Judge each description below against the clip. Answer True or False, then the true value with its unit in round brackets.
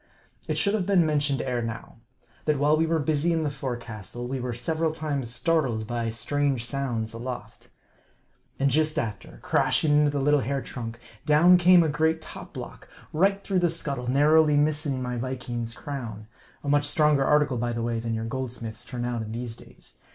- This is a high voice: False (140 Hz)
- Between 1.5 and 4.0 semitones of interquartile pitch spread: False (4.4 semitones)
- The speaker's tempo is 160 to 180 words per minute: False (190 wpm)